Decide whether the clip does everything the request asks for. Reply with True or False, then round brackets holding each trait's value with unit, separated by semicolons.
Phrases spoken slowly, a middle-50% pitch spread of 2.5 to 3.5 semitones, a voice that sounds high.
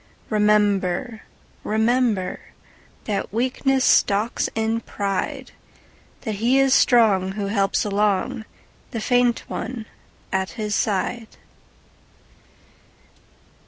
True (75 wpm; 3.0 semitones; 215 Hz)